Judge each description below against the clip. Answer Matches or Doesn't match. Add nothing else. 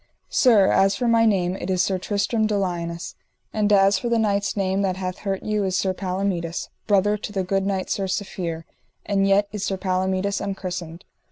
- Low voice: Doesn't match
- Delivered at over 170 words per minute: Matches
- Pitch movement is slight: Matches